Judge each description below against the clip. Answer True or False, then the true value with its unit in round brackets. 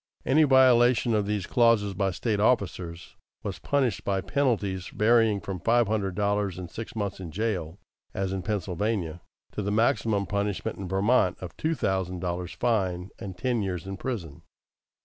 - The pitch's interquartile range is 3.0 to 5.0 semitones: True (3.6 semitones)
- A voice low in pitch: True (100 Hz)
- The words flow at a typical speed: True (165 wpm)